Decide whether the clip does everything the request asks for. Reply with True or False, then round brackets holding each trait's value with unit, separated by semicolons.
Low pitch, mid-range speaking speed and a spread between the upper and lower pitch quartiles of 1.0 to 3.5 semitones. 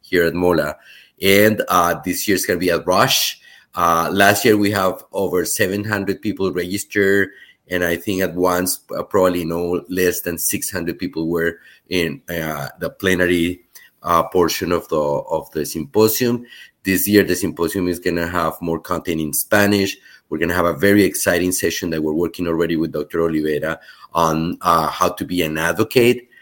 True (90 Hz; 185 wpm; 2.8 semitones)